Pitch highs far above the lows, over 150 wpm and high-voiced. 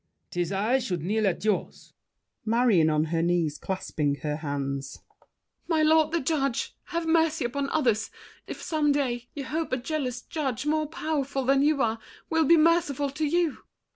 Yes: wide, 8.1 semitones; average, 170 wpm; very high, 265 Hz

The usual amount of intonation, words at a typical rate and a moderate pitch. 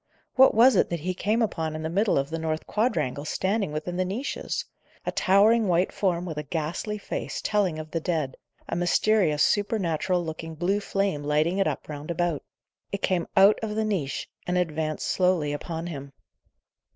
Yes: average, 4.2 semitones; average, 185 wpm; medium, 175 Hz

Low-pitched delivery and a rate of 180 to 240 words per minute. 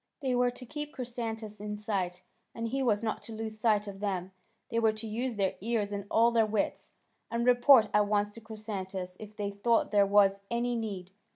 No: high, 215 Hz; fast, 205 wpm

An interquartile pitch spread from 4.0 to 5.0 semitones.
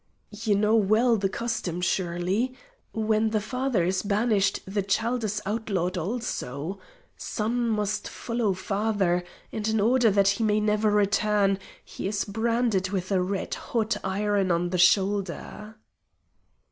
No: narrow, 2.5 semitones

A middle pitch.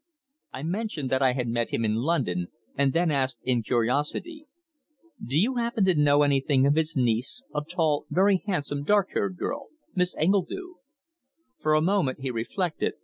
Yes: medium, 150 Hz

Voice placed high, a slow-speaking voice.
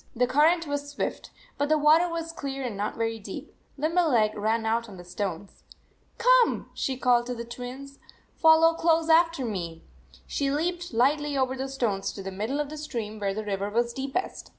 No: very high, 265 Hz; average, 195 wpm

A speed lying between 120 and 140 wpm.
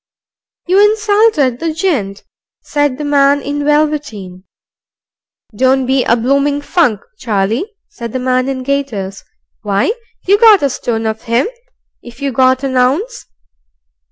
Yes: slow, 135 wpm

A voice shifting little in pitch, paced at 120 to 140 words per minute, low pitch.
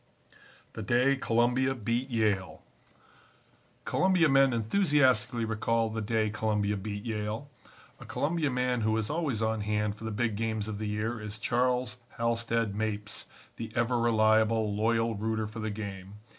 No: narrow, 2.3 semitones; average, 150 wpm; low, 110 Hz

